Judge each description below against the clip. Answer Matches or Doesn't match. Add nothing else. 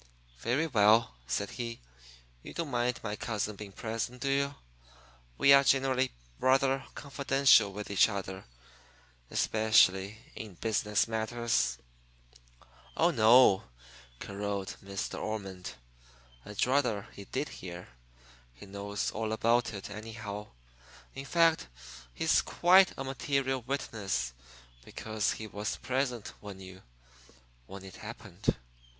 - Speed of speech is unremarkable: Doesn't match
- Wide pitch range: Doesn't match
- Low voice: Matches